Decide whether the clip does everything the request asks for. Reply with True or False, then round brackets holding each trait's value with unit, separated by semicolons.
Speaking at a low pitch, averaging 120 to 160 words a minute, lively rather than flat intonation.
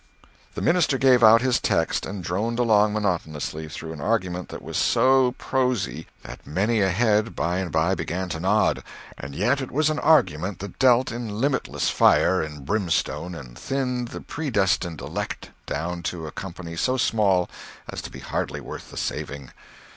False (100 Hz; 170 wpm; 6.6 semitones)